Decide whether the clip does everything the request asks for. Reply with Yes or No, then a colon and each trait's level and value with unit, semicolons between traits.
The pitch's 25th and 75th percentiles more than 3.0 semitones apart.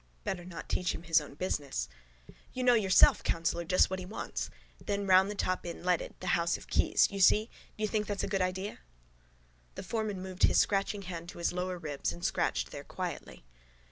No: average, 2.7 semitones